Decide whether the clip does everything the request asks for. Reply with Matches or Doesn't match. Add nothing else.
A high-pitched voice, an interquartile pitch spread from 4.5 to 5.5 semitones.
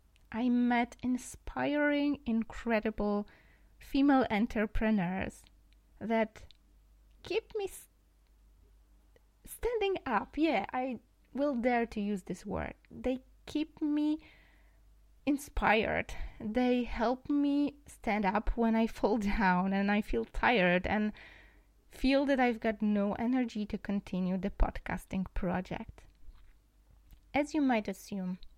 Matches